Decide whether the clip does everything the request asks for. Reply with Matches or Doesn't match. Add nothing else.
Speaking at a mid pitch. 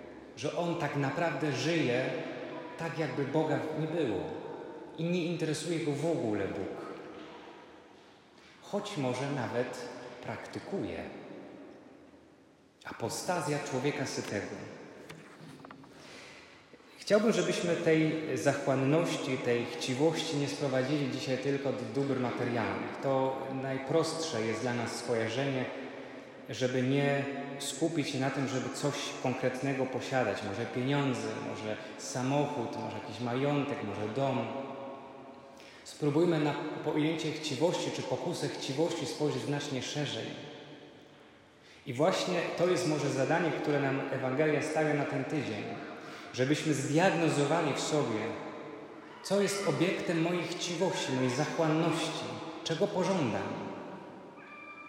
Matches